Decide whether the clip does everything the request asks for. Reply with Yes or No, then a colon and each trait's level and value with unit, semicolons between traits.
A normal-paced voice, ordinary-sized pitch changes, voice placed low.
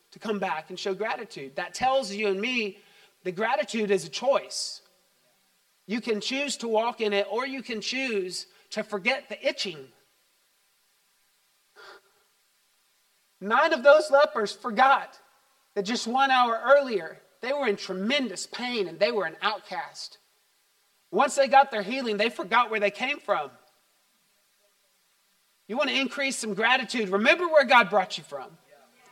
No: average, 150 wpm; average, 3.6 semitones; high, 200 Hz